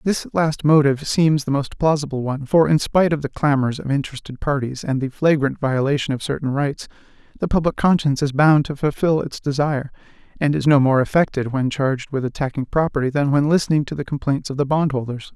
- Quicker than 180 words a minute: Yes, fast, 205 wpm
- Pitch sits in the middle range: Yes, medium, 145 Hz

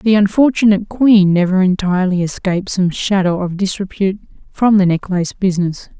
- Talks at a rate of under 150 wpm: Yes, average, 140 wpm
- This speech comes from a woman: Yes, female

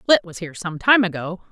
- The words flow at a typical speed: No, fast, 235 wpm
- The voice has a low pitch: No, medium, 185 Hz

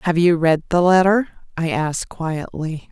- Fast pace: No, average, 165 wpm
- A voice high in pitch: No, medium, 170 Hz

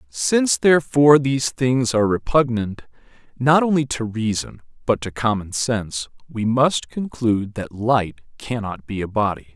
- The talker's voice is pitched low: Yes, low, 120 Hz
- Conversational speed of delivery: Yes, average, 145 wpm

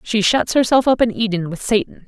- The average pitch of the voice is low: No, high, 215 Hz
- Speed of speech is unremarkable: No, fast, 230 wpm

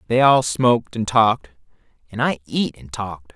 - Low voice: Yes, low, 110 Hz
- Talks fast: No, average, 180 wpm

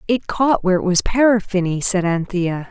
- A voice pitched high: Yes, high, 195 Hz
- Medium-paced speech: Yes, average, 180 wpm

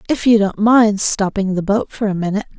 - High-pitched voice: Yes, high, 205 Hz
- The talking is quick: Yes, fast, 230 wpm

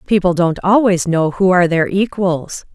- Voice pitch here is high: No, medium, 180 Hz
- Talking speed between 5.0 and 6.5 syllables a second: No, 4.7 syllables/s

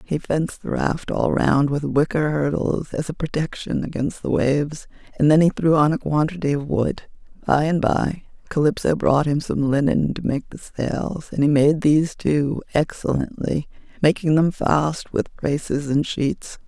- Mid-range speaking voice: Yes, medium, 150 Hz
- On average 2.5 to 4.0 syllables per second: No, 4.5 syllables/s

